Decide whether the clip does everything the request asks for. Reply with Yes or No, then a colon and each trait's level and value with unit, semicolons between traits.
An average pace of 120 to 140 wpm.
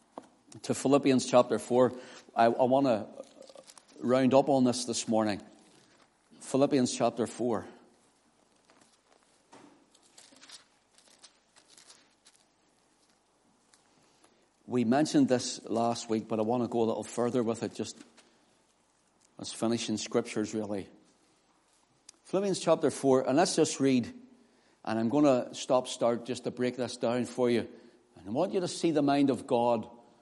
Yes: slow, 135 wpm